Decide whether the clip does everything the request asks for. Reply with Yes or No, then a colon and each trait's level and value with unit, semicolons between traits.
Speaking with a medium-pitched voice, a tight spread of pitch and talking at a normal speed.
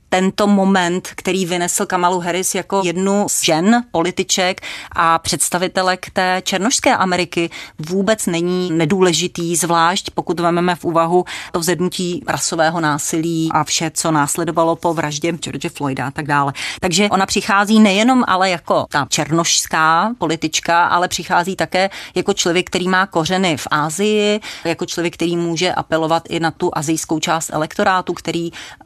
Yes: medium, 175 Hz; narrow, 2.2 semitones; average, 145 wpm